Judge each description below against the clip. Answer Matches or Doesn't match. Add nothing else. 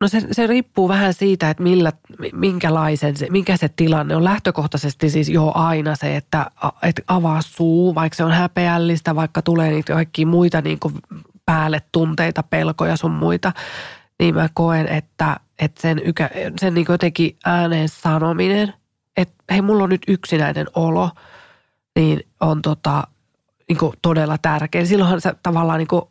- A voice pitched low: Doesn't match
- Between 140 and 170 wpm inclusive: Matches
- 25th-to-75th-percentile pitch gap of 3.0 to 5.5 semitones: Doesn't match